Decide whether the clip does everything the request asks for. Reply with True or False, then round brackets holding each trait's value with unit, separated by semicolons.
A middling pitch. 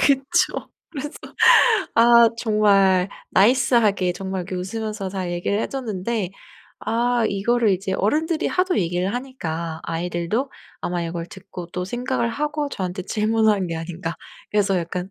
False (200 Hz)